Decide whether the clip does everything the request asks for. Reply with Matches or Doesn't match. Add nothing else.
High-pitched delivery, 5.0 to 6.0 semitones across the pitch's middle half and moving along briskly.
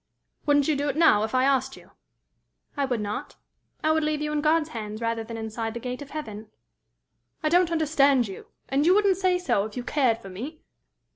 Matches